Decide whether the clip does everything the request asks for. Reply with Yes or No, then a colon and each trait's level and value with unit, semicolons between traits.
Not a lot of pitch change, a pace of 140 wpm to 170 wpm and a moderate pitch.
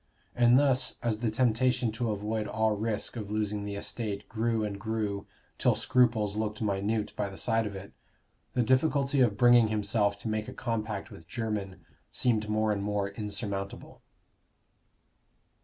No: narrow, 2.2 semitones; average, 155 wpm; low, 110 Hz